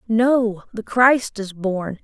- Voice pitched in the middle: No, high, 215 Hz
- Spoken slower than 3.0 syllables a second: Yes, 2.8 syllables/s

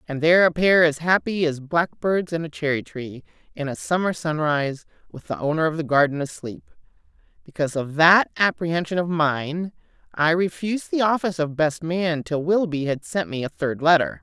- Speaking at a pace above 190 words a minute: No, average, 185 wpm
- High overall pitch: No, medium, 160 Hz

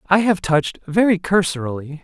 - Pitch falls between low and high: Yes, medium, 175 Hz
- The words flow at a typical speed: Yes, average, 145 wpm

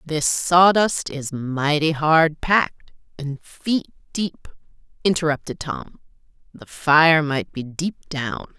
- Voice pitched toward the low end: No, medium, 155 Hz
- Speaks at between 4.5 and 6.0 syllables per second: No, 3.3 syllables/s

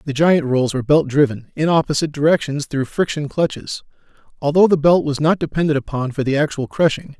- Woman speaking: No, male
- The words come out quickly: No, average, 190 wpm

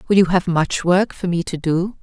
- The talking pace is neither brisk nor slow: No, fast, 265 wpm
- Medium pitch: Yes, medium, 180 Hz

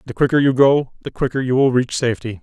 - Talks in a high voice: No, low, 130 Hz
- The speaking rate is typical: No, fast, 250 wpm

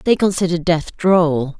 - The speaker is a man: No, female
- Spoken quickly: No, average, 150 wpm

